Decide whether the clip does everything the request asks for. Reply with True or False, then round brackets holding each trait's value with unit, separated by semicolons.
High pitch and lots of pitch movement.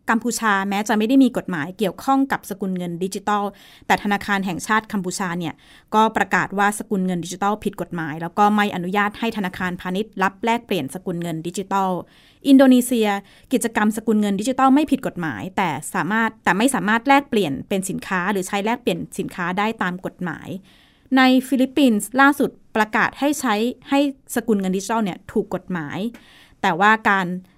False (205 Hz; 3.9 semitones)